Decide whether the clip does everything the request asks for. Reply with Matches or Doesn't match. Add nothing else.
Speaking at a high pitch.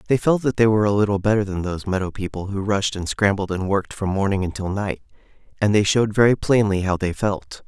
Doesn't match